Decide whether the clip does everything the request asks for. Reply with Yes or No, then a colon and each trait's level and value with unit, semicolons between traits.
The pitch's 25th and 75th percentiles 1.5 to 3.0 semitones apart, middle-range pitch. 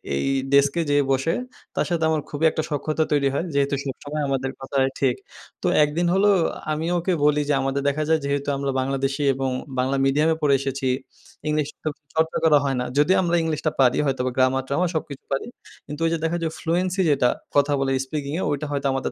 Yes: narrow, 2.6 semitones; medium, 145 Hz